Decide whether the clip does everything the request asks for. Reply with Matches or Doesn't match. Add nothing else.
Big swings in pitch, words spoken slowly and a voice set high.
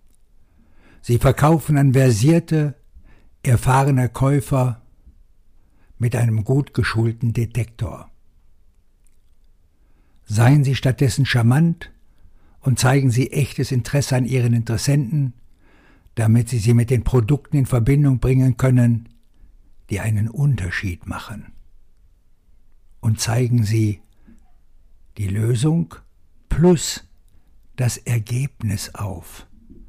Doesn't match